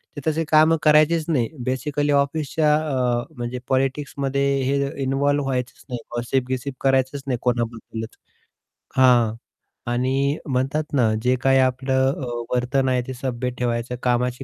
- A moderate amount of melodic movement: No, narrow, 2.2 semitones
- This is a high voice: No, low, 130 Hz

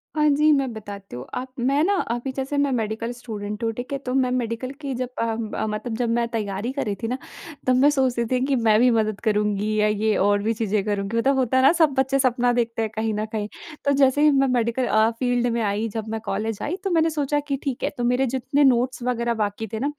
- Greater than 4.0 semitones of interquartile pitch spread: No, average, 3.4 semitones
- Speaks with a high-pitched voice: Yes, high, 240 Hz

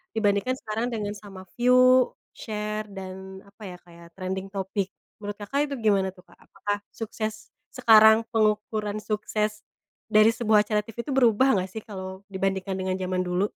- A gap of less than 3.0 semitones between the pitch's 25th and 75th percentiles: Yes, narrow, 2.4 semitones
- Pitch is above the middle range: Yes, high, 210 Hz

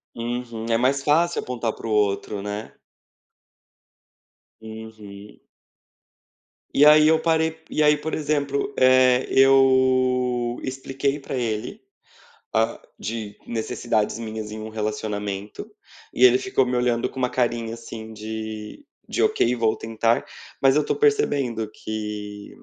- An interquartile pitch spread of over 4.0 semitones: No, average, 3.6 semitones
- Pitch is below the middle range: Yes, low, 120 Hz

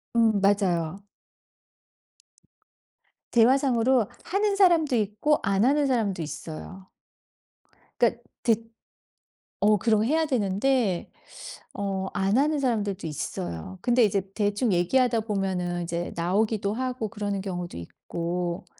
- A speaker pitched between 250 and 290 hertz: No, high, 205 Hz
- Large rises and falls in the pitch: No, average, 4.6 semitones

